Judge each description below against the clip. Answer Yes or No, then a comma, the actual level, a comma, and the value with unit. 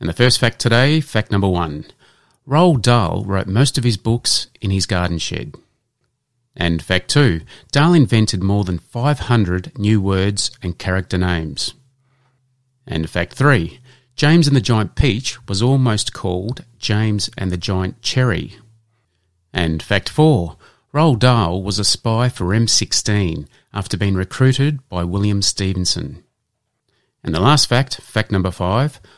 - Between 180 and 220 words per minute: No, average, 145 wpm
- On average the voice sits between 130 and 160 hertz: No, low, 110 Hz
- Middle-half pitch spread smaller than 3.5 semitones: No, wide, 5.4 semitones